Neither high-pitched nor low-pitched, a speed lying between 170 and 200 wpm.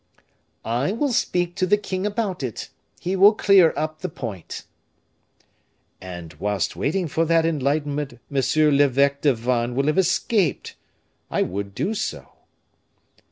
No: medium, 150 Hz; average, 140 wpm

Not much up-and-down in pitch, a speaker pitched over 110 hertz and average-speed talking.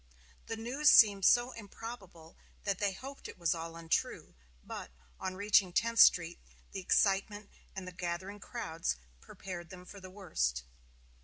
No: average, 3.4 semitones; high, 190 Hz; average, 150 wpm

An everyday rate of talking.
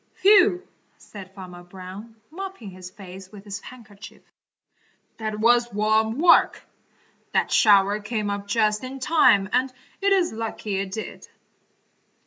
No: slow, 130 wpm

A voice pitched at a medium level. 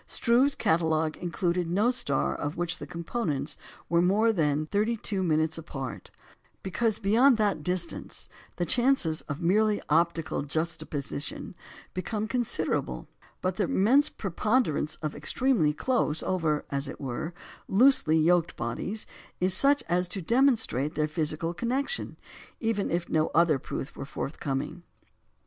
Yes: medium, 175 Hz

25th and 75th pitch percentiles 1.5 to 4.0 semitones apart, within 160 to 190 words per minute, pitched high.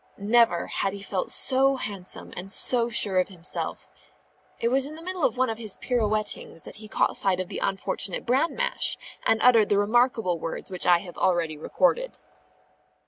No: average, 5.2 semitones; average, 185 wpm; high, 215 Hz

